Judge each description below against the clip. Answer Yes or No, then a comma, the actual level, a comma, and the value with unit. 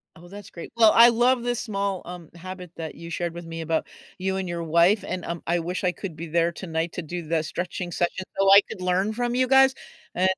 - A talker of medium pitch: Yes, medium, 180 Hz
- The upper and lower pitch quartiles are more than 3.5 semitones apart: No, average, 2.9 semitones